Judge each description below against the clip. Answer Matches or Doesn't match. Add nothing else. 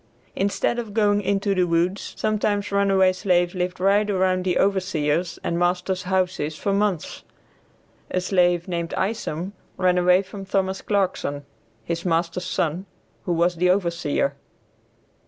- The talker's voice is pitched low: Doesn't match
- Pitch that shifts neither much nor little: Doesn't match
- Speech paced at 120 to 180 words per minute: Matches